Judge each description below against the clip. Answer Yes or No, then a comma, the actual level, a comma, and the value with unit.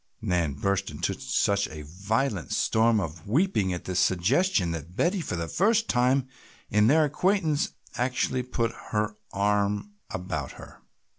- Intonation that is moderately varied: No, wide, 7.4 semitones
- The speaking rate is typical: Yes, average, 145 wpm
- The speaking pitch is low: Yes, low, 105 Hz